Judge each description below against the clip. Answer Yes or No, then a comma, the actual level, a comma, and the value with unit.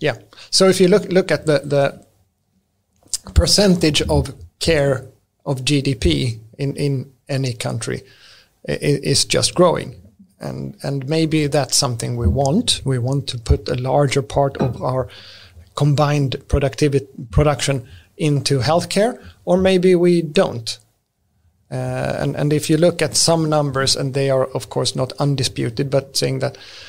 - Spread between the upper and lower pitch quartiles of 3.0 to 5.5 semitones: Yes, average, 4.4 semitones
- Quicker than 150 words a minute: No, average, 145 wpm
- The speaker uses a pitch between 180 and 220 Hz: No, low, 135 Hz